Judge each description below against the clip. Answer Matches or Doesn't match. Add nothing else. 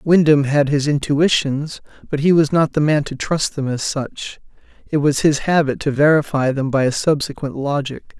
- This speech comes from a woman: Doesn't match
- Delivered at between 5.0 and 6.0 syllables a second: Doesn't match